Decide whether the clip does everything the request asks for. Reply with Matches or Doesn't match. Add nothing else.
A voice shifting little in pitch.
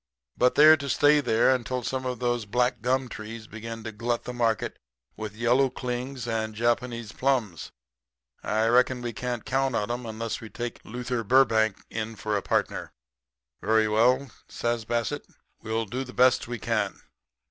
Matches